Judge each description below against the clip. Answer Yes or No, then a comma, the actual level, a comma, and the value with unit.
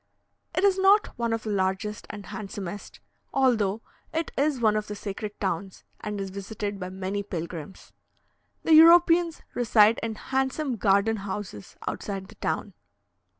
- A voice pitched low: No, high, 210 Hz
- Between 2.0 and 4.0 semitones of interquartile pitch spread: No, average, 4.8 semitones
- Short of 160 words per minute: Yes, average, 150 wpm